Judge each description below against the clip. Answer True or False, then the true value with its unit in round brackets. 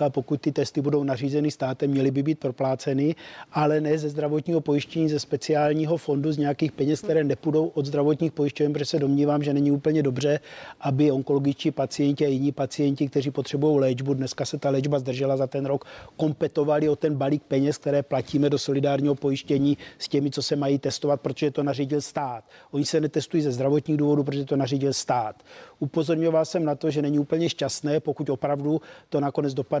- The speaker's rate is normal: False (190 wpm)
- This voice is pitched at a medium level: True (145 Hz)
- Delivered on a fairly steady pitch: True (1.3 semitones)